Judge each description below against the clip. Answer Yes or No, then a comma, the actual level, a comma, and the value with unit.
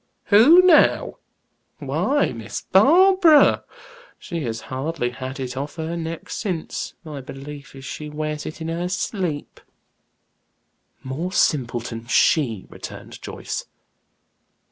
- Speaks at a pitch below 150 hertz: No, medium, 155 Hz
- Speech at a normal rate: No, slow, 115 wpm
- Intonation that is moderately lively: No, wide, 5.8 semitones